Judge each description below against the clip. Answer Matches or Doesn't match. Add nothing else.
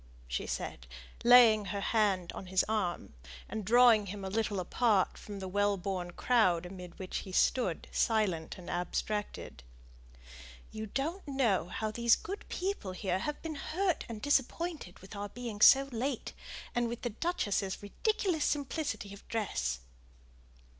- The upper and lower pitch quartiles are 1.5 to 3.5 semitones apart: Doesn't match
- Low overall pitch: Doesn't match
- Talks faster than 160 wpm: Doesn't match